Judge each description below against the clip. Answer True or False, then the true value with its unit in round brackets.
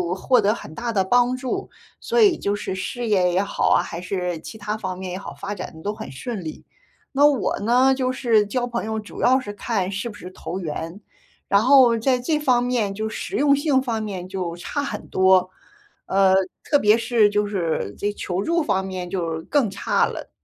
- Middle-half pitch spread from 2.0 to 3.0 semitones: False (4.7 semitones)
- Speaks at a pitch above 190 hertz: True (210 Hz)